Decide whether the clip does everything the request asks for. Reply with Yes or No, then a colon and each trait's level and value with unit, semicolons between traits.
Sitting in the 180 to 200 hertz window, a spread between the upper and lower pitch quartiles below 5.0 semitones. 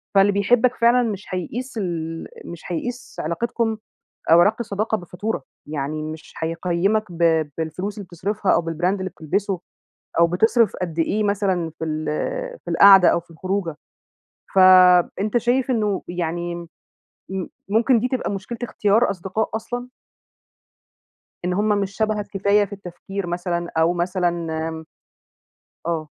Yes: high, 190 Hz; average, 3.7 semitones